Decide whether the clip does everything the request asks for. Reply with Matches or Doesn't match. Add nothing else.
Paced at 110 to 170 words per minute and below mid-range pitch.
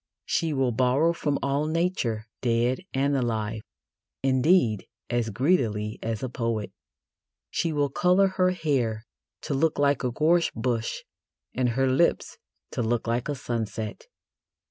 Matches